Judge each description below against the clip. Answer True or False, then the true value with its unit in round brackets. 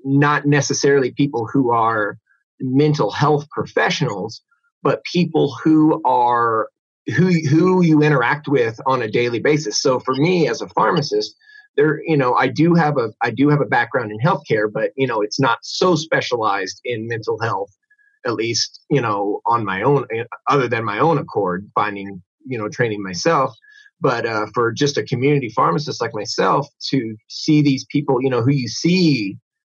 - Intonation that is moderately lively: False (5.8 semitones)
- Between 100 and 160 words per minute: False (175 wpm)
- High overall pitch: False (140 Hz)